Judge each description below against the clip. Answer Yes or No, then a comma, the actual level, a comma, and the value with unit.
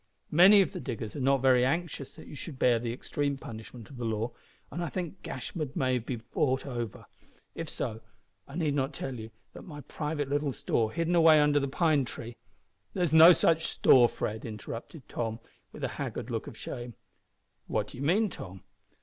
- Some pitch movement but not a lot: Yes, average, 4.8 semitones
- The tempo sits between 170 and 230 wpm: Yes, average, 200 wpm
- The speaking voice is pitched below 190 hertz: Yes, low, 135 Hz